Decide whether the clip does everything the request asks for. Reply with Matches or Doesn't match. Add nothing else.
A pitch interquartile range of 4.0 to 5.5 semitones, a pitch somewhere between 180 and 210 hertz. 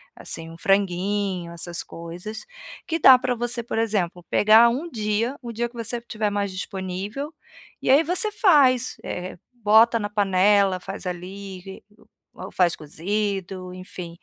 Matches